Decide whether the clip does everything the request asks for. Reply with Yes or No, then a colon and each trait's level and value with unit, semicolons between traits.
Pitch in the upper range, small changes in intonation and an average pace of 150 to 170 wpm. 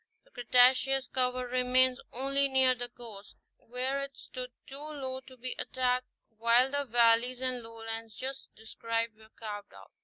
Yes: very high, 250 Hz; narrow, 2.2 semitones; average, 155 wpm